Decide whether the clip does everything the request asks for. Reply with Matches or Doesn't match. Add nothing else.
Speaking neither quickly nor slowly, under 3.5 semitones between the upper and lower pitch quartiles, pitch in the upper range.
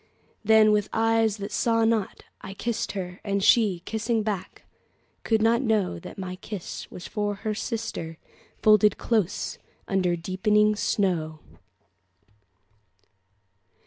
Doesn't match